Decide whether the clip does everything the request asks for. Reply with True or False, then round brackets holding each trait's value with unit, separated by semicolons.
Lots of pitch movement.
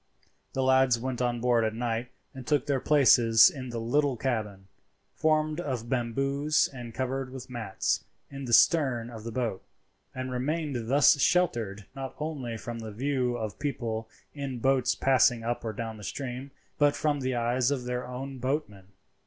False (2.9 semitones)